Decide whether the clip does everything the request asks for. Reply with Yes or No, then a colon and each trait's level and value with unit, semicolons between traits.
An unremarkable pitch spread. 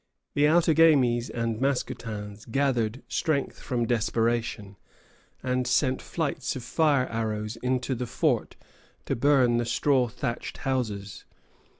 Yes: average, 3.2 semitones